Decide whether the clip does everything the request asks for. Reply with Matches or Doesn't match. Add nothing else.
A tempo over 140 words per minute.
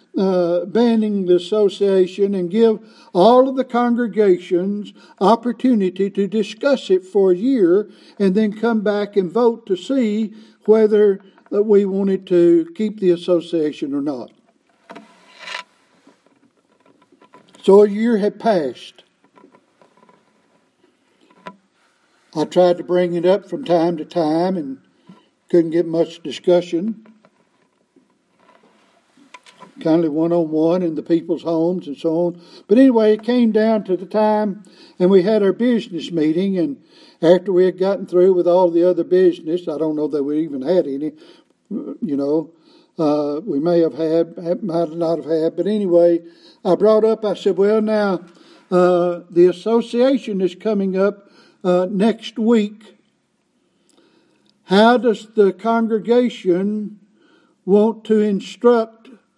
Doesn't match